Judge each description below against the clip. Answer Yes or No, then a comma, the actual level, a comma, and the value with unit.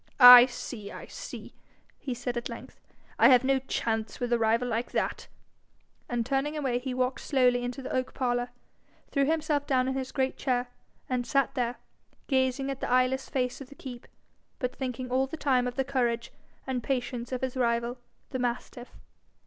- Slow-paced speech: No, average, 185 wpm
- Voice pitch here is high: Yes, very high, 255 Hz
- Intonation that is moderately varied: No, narrow, 1.5 semitones